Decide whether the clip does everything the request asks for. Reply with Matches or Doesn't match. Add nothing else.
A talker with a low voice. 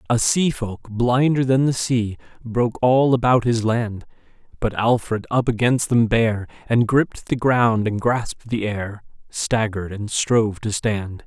Matches